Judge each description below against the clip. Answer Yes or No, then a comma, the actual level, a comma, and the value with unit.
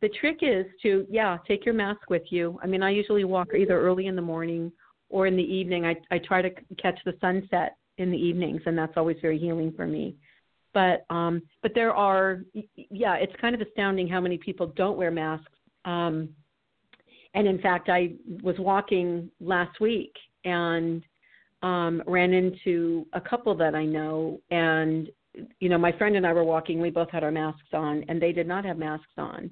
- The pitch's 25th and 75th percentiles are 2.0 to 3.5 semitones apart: Yes, narrow, 2.4 semitones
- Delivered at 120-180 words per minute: No, average, 195 wpm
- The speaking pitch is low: No, medium, 180 Hz